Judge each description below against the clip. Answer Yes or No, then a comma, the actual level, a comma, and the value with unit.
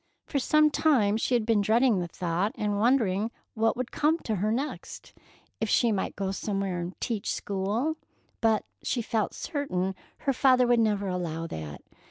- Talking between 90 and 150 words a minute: No, average, 170 wpm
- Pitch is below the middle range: No, high, 215 Hz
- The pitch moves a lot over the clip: No, average, 4.4 semitones